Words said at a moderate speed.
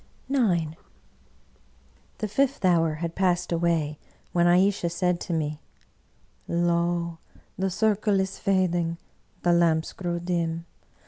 No: slow, 120 wpm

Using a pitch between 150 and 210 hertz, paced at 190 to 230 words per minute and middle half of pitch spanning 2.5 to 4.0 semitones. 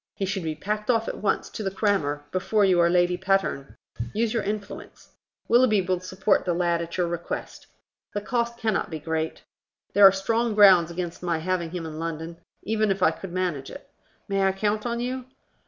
Yes: high, 190 Hz; average, 200 wpm; average, 3.7 semitones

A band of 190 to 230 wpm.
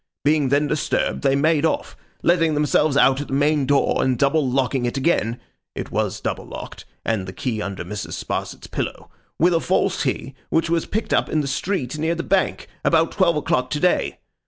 Yes: average, 200 wpm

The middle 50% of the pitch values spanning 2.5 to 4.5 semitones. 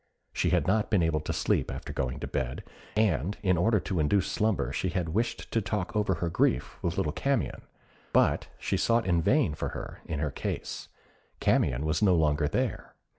No: wide, 5.6 semitones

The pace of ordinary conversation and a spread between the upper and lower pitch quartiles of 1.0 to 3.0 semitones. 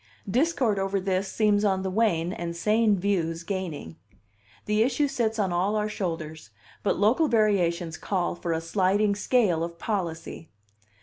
No: average, 150 wpm; average, 3.9 semitones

